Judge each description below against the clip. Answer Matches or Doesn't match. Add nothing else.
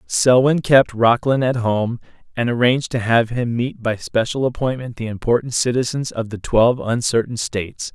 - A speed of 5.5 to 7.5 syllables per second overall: Doesn't match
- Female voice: Doesn't match